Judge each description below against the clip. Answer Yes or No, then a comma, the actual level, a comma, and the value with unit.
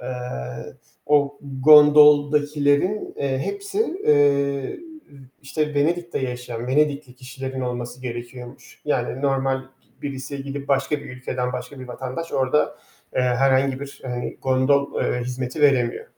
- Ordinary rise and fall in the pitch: No, narrow, 2.2 semitones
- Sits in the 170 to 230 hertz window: No, low, 135 Hz